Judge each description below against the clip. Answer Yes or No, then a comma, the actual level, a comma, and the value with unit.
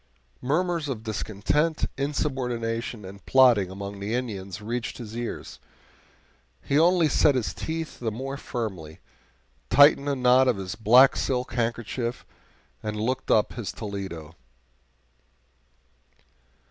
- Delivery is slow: Yes, slow, 120 wpm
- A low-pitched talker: Yes, low, 120 Hz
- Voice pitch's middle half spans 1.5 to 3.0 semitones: No, average, 4.3 semitones